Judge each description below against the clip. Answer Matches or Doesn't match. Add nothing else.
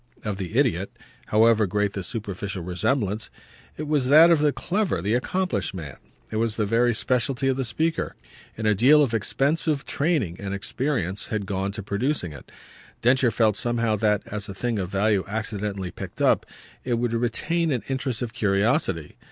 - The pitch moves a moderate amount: Matches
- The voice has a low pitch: Matches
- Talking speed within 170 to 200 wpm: Matches